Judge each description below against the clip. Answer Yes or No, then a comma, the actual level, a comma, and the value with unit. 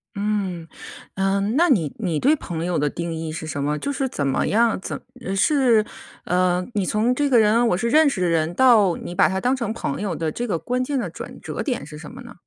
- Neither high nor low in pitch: No, high, 200 Hz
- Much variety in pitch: Yes, wide, 6.3 semitones